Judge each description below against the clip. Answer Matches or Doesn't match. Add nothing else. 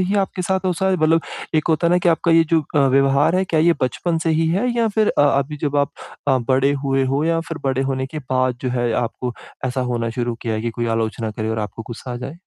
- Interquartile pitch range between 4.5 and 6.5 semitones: Matches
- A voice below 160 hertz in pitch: Matches